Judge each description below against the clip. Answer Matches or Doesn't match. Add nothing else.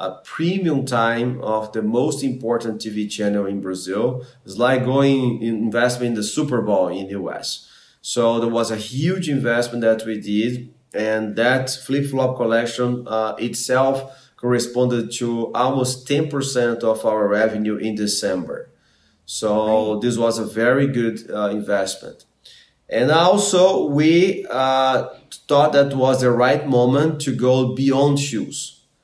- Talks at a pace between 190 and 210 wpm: Doesn't match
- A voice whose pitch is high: Doesn't match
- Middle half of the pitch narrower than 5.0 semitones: Matches